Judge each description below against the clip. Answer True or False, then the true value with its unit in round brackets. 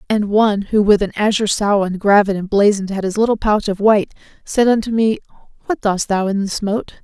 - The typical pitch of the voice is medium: False (205 Hz)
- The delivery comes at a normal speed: False (215 wpm)